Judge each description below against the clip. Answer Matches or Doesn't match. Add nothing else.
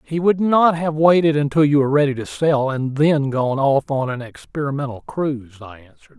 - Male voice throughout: Matches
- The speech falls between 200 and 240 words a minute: Matches